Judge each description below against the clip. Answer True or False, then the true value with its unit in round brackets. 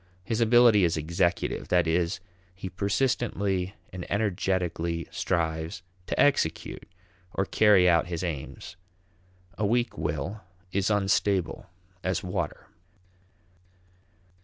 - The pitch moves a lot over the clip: False (3.3 semitones)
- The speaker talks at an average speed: False (105 wpm)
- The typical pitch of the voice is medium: False (90 Hz)